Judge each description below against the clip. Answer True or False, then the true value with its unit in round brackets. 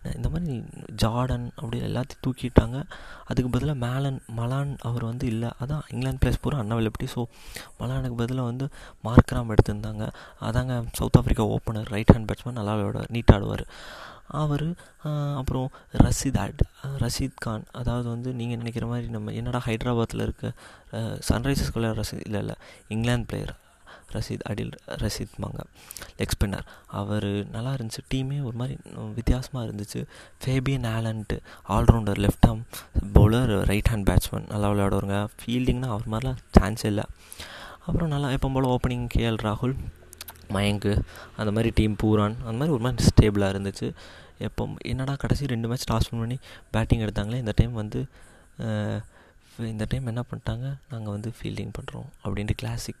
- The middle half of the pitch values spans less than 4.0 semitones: True (3.2 semitones)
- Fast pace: True (140 wpm)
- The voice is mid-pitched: False (115 Hz)